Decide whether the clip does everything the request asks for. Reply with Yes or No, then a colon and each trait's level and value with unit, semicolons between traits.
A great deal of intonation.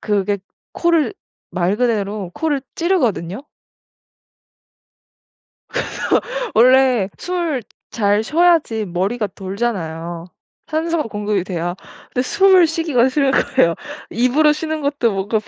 Yes: wide, 7.4 semitones